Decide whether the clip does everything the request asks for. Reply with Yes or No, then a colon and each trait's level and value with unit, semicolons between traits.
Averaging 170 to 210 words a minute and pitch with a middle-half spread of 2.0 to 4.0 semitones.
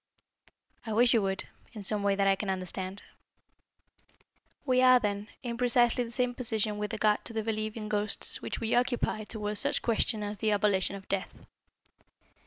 Yes: average, 180 wpm; narrow, 2.5 semitones